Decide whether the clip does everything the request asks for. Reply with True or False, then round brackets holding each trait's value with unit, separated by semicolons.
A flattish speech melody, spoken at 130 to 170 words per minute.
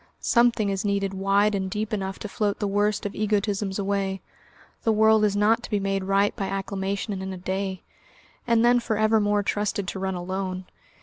False (1.6 semitones; 200 wpm)